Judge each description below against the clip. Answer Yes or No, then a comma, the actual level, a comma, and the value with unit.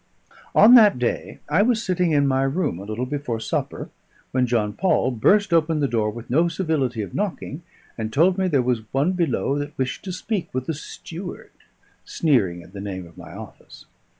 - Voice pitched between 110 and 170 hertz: Yes, medium, 140 Hz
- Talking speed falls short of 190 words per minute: No, average, 195 wpm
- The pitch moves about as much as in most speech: No, wide, 7.0 semitones